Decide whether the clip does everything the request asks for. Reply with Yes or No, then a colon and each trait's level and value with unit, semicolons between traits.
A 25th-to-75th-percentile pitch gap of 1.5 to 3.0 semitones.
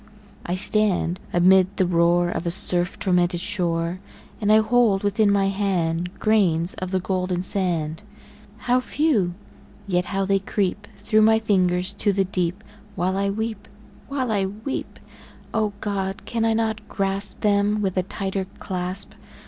Yes: narrow, 2.6 semitones